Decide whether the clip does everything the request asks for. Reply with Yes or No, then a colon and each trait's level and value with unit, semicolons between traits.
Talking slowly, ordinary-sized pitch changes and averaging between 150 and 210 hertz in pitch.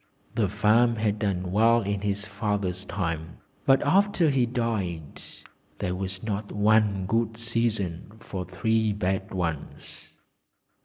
No: slow, 125 wpm; average, 3.4 semitones; low, 105 Hz